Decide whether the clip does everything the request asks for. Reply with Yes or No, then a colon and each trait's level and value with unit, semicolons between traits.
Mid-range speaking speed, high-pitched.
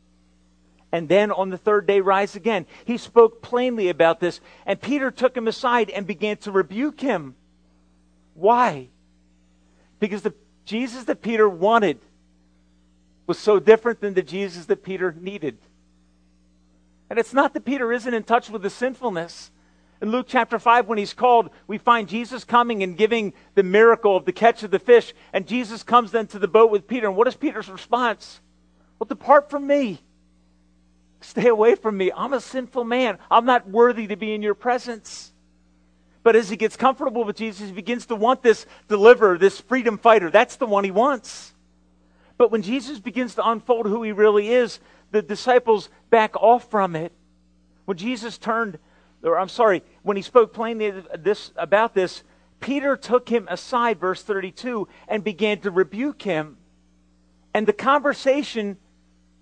Yes: average, 170 wpm; high, 210 Hz